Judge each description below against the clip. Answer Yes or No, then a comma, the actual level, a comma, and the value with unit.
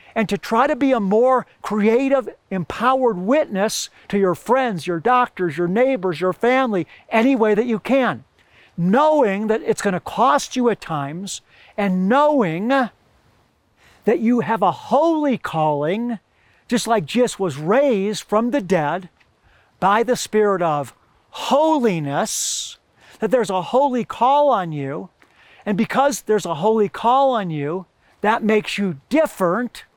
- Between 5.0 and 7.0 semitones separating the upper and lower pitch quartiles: Yes, wide, 5.4 semitones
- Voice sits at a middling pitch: No, high, 220 Hz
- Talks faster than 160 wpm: No, average, 145 wpm